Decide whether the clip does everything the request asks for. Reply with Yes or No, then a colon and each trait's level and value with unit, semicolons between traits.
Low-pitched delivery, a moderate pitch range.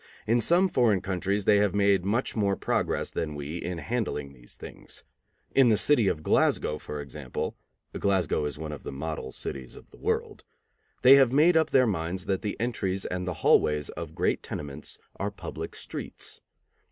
No: very low, 95 Hz; wide, 6.9 semitones